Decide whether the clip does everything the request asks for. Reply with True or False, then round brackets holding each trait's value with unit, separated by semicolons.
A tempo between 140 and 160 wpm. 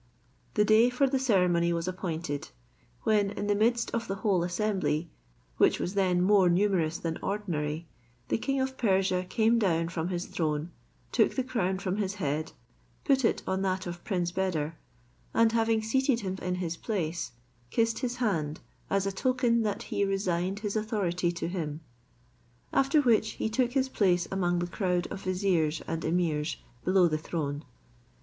False (170 wpm)